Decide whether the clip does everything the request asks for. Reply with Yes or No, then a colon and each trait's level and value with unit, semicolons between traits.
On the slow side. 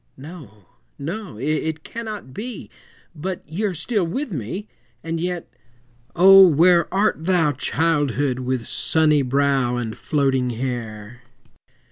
Yes: slow, 120 wpm